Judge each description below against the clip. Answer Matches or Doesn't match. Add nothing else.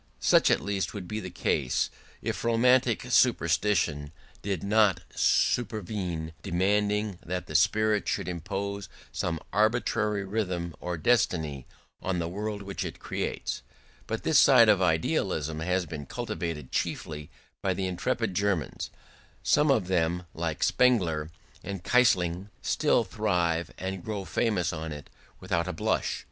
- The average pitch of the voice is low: Matches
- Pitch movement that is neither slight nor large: Matches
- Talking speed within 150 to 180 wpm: Doesn't match